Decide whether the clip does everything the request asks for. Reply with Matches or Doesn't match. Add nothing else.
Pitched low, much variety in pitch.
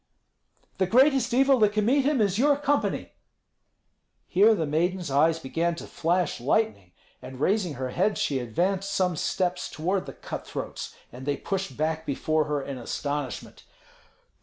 Doesn't match